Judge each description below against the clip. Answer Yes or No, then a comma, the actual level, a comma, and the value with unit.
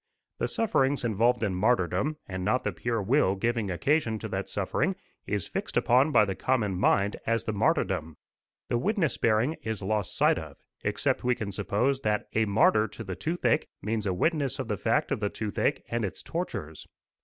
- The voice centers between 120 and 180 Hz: No, low, 110 Hz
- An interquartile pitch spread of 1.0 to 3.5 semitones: No, average, 4.4 semitones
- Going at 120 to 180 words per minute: No, average, 190 wpm